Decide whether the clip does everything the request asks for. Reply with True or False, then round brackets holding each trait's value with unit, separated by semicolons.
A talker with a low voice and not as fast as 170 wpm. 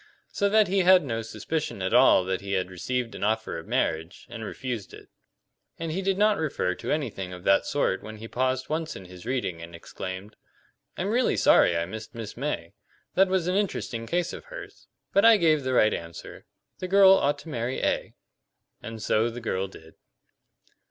False (120 Hz; 200 wpm)